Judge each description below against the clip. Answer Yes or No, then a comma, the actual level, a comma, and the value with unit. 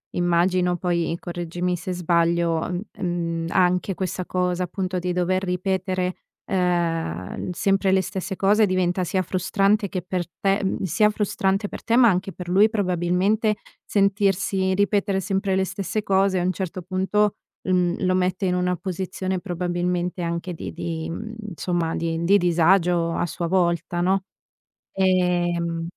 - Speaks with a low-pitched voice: No, medium, 180 Hz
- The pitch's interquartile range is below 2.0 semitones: Yes, narrow, 1.6 semitones